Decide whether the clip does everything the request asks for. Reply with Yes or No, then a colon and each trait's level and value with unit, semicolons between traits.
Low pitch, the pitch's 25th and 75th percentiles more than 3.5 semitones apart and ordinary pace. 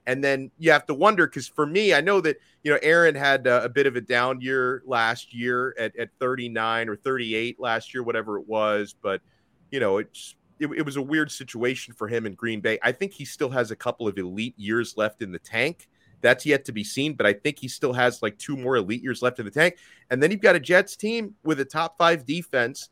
No: low, 130 Hz; average, 4.3 semitones; fast, 250 wpm